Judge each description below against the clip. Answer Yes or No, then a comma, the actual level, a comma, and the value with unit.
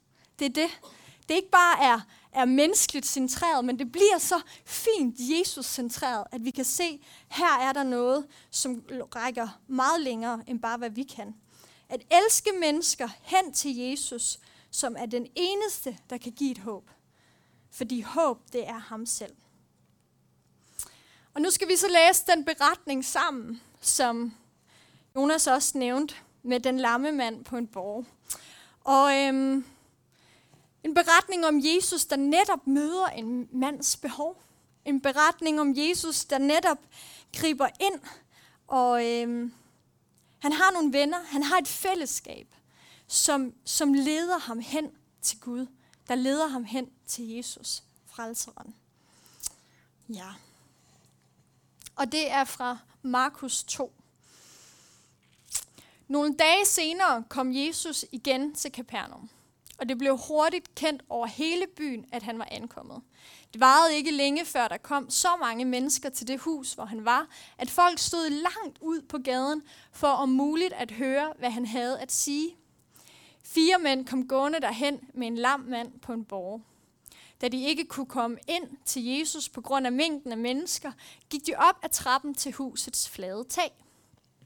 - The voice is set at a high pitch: Yes, very high, 275 Hz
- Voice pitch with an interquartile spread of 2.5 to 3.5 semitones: No, average, 4.3 semitones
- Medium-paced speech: Yes, average, 155 wpm